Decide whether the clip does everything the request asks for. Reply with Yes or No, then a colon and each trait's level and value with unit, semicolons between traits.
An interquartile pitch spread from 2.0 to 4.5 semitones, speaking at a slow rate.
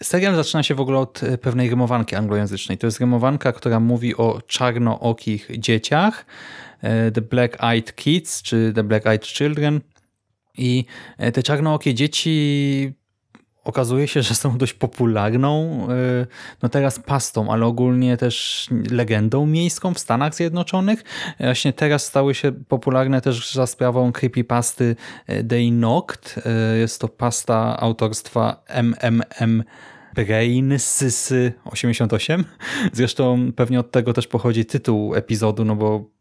No: average, 3.1 semitones; average, 125 wpm